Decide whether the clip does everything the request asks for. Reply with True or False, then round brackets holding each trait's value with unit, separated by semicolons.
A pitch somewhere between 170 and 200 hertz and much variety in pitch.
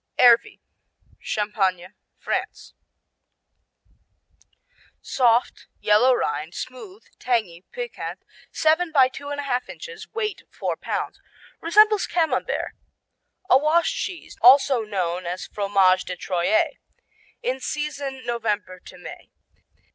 False (250 Hz; 7.6 semitones)